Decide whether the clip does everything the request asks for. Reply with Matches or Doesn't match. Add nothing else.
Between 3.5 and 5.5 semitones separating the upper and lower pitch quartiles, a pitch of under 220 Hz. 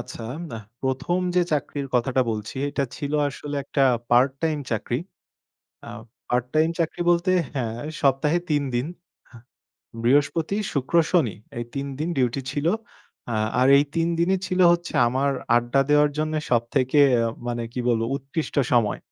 Matches